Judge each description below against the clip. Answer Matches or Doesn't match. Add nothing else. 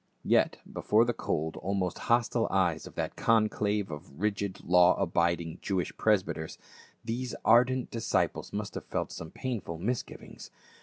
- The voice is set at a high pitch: Doesn't match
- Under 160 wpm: Matches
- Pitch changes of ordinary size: Matches